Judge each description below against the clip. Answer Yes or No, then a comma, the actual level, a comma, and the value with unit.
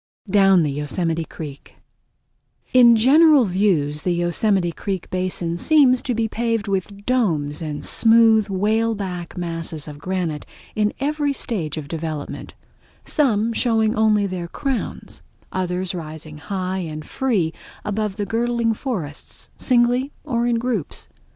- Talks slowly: Yes, slow, 125 wpm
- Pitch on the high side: Yes, high, 195 Hz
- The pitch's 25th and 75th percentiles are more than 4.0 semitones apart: Yes, wide, 5.5 semitones